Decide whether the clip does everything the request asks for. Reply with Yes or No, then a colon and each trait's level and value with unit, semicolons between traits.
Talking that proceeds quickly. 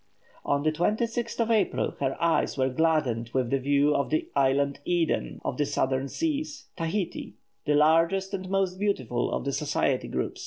No: average, 170 wpm